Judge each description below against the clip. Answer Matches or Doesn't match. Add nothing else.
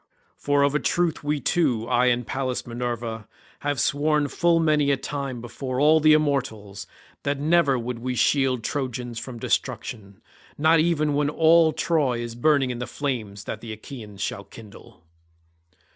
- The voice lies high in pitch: Doesn't match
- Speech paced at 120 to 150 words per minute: Doesn't match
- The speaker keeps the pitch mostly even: Doesn't match